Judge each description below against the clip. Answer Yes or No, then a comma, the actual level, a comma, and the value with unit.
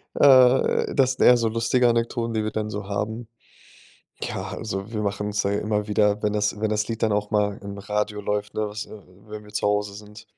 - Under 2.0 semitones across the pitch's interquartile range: Yes, narrow, 1.4 semitones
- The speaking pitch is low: Yes, low, 105 Hz